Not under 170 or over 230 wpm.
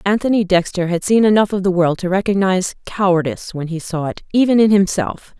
Yes: average, 200 wpm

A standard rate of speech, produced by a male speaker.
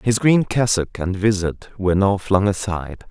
Yes: average, 175 wpm; male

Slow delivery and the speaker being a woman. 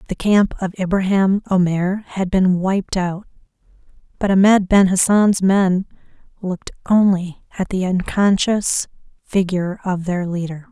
Yes: slow, 130 wpm; female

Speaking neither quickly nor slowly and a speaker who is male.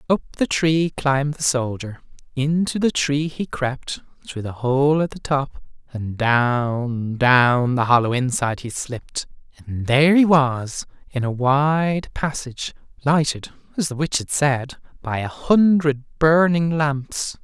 Yes: average, 150 wpm; male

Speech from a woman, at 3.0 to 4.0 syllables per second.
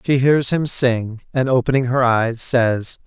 No: male; 3.9 syllables/s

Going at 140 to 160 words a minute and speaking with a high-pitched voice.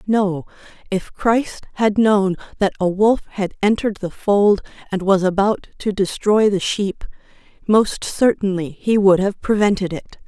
Yes: average, 150 wpm; high, 200 Hz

